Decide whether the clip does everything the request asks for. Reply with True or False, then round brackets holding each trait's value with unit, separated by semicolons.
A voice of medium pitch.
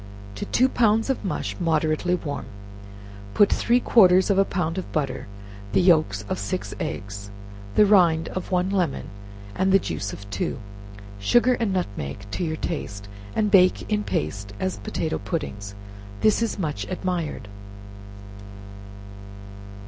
True (175 Hz)